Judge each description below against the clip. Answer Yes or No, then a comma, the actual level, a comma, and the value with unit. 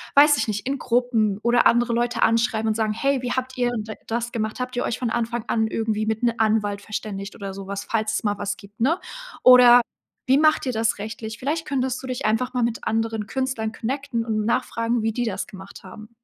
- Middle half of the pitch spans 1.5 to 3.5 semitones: Yes, narrow, 2.5 semitones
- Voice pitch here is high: Yes, high, 230 Hz